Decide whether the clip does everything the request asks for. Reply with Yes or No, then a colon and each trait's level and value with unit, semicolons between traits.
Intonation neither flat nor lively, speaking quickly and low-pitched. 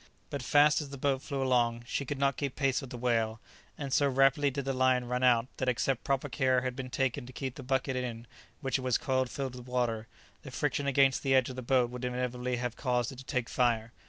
No: narrow, 1.7 semitones; fast, 245 wpm; low, 130 Hz